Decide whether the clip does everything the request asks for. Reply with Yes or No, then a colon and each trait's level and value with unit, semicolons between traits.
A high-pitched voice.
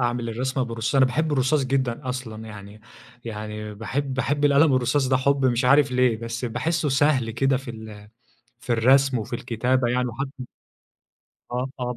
No: low, 125 Hz